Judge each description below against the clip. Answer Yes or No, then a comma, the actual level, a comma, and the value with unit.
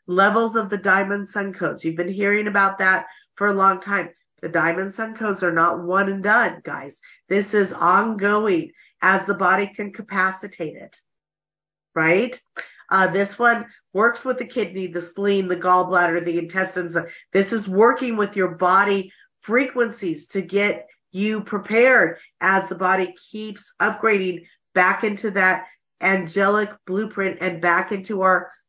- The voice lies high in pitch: Yes, high, 195 Hz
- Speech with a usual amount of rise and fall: No, narrow, 2.3 semitones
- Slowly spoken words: No, average, 155 wpm